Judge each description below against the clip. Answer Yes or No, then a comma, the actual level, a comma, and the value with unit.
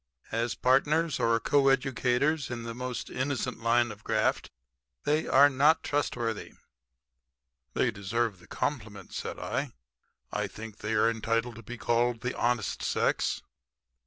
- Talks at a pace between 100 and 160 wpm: Yes, slow, 135 wpm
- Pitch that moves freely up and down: No, average, 3.0 semitones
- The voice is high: No, low, 120 Hz